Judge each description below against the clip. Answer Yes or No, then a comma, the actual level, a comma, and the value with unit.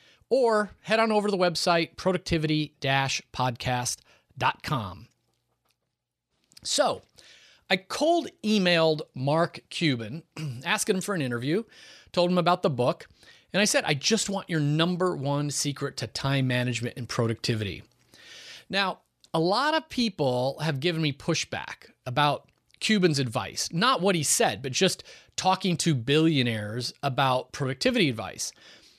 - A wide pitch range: Yes, wide, 6.5 semitones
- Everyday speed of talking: No, slow, 130 wpm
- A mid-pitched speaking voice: Yes, medium, 155 Hz